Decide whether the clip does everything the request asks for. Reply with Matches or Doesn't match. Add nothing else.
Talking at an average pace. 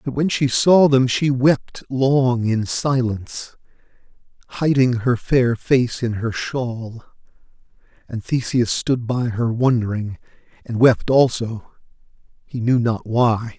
Doesn't match